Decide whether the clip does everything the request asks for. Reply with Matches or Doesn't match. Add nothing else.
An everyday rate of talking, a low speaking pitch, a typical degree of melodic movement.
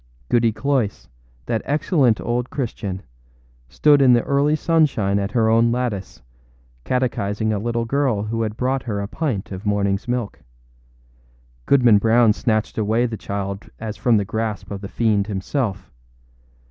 Matches